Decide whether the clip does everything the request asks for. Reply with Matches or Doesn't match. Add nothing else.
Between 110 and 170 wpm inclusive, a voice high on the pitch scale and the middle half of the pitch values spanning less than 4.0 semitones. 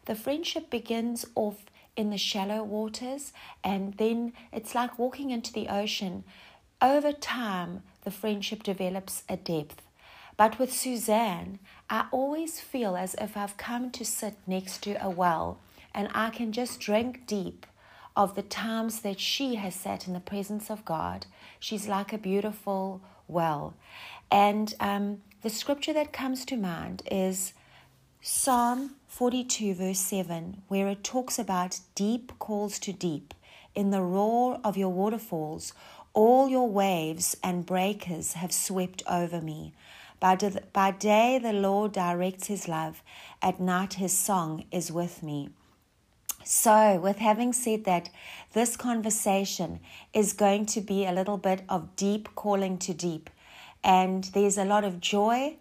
Matches